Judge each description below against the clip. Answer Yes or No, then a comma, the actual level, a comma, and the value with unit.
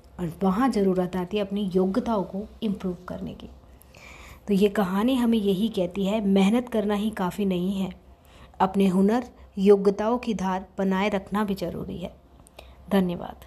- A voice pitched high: Yes, high, 200 Hz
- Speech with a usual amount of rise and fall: No, narrow, 2.1 semitones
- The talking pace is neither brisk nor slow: Yes, average, 155 wpm